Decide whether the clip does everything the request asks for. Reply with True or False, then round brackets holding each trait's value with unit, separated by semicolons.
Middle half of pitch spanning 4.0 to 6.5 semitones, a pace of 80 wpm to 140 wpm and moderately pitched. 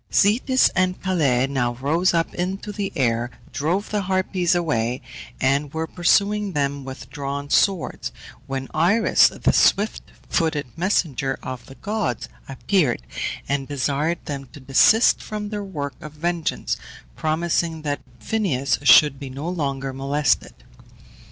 True (5.3 semitones; 135 wpm; 155 Hz)